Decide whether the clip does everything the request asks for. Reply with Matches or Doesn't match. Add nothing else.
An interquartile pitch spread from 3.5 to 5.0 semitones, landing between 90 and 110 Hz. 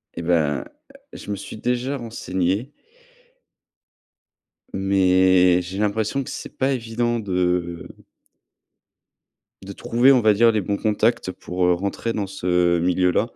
Matches